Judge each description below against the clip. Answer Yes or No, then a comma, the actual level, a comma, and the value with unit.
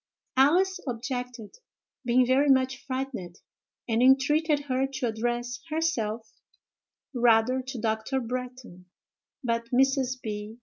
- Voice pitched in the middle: No, very high, 250 Hz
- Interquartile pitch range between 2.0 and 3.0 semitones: Yes, narrow, 2.4 semitones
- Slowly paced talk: Yes, slow, 105 wpm